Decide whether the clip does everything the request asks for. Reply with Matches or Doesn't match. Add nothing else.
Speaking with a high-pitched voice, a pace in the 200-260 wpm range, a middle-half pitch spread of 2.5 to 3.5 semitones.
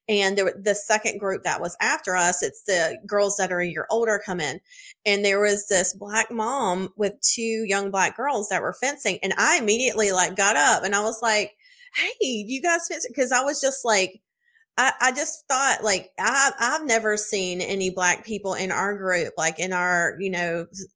Doesn't match